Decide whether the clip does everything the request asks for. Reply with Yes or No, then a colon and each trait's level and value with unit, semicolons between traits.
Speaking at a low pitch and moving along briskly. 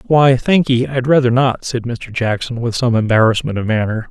No: low, 120 Hz; average, 190 wpm